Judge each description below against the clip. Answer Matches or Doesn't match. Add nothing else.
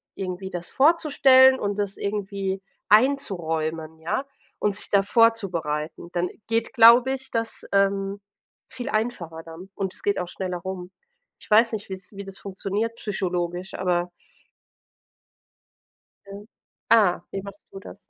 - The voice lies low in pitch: Doesn't match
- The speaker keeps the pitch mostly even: Doesn't match